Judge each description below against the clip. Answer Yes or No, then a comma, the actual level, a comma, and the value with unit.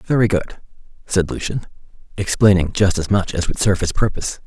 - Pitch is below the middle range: Yes, very low, 95 Hz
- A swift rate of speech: No, average, 175 wpm